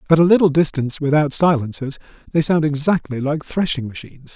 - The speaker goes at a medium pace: Yes, average, 165 wpm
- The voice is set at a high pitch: No, medium, 150 Hz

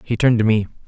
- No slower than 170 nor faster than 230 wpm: No, fast, 275 wpm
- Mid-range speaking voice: No, low, 110 Hz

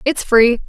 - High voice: Yes, high, 245 Hz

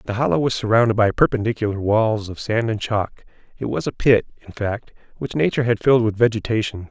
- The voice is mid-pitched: No, low, 110 Hz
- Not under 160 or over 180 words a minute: No, average, 200 wpm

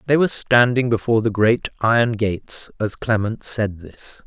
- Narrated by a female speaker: No, male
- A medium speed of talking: Yes, average, 170 wpm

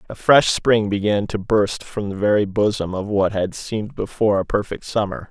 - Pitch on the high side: No, low, 105 Hz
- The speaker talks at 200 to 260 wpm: Yes, fast, 205 wpm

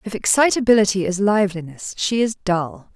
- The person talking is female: Yes, female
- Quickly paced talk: No, average, 140 wpm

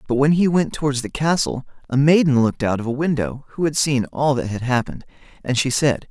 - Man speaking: Yes, male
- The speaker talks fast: Yes, fast, 235 wpm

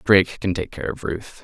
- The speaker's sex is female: No, male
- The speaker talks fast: Yes, fast, 250 wpm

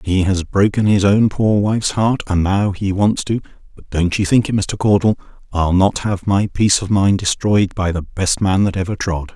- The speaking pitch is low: Yes, low, 100 Hz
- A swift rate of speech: Yes, fast, 220 wpm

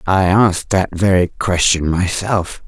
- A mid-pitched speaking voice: No, very low, 95 Hz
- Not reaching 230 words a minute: Yes, slow, 135 wpm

